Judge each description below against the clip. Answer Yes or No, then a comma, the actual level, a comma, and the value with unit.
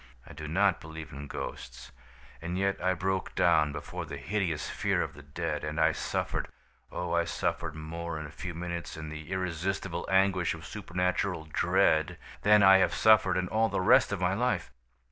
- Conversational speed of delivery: Yes, average, 185 wpm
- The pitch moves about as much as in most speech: Yes, average, 3.3 semitones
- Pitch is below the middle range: Yes, very low, 85 Hz